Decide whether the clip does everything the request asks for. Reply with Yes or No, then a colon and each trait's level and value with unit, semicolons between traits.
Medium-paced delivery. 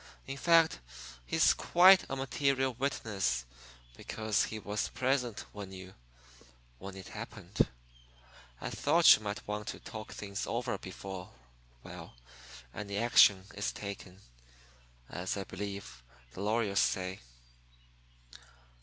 No: slow, 120 wpm